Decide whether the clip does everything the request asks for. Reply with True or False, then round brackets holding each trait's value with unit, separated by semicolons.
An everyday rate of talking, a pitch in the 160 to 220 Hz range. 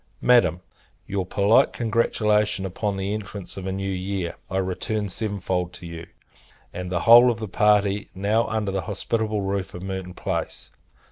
False (165 wpm; 100 Hz)